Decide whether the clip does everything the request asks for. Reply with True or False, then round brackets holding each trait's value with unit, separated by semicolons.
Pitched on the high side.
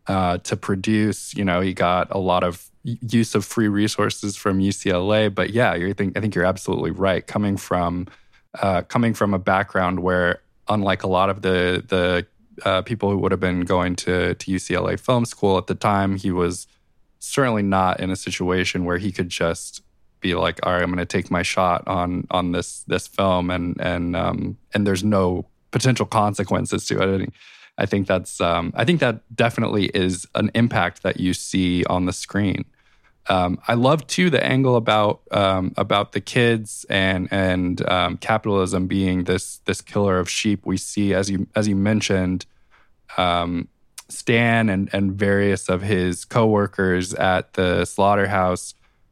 False (95 Hz)